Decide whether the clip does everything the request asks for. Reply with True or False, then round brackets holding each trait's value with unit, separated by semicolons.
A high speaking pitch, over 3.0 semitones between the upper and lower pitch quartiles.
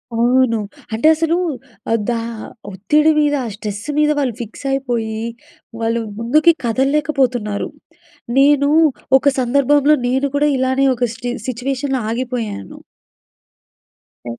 True (255 Hz; 3.6 semitones)